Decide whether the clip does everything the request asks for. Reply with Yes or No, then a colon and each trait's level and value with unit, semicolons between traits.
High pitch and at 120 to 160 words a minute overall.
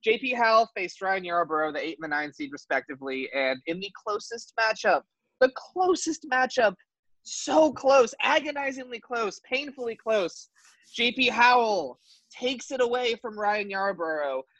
Yes: high, 230 Hz; average, 140 wpm